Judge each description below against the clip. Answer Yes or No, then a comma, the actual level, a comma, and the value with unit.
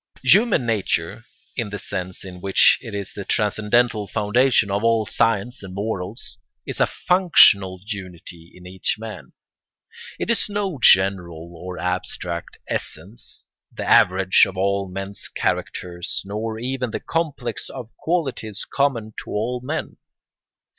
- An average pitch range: Yes, average, 4.5 semitones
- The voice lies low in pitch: Yes, low, 105 Hz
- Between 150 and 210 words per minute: No, average, 140 wpm